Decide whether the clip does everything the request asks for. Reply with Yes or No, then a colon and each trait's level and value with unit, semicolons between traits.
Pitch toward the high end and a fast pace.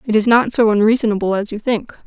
Yes: high, 220 Hz; fast, 230 wpm